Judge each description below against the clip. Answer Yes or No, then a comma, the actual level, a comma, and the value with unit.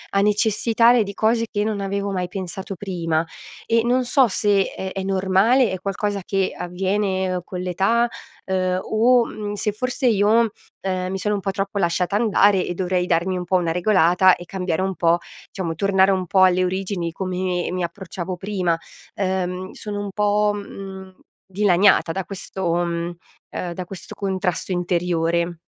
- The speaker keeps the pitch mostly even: Yes, narrow, 2.2 semitones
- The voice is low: No, high, 190 Hz